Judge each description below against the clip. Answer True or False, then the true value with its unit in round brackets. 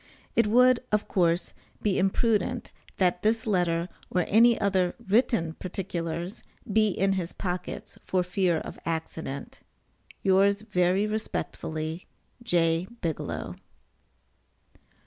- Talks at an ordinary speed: False (110 wpm)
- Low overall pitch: False (185 Hz)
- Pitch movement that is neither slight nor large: True (3.7 semitones)